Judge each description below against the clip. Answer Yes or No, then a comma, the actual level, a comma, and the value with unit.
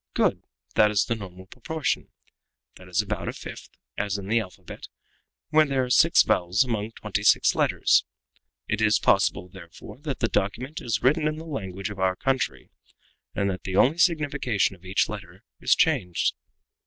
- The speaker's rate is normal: Yes, average, 175 wpm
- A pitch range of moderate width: No, wide, 6.0 semitones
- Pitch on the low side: Yes, low, 110 Hz